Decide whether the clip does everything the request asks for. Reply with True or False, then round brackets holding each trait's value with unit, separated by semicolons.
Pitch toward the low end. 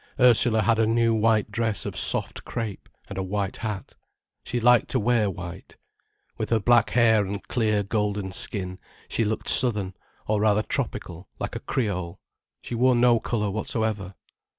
True (110 Hz)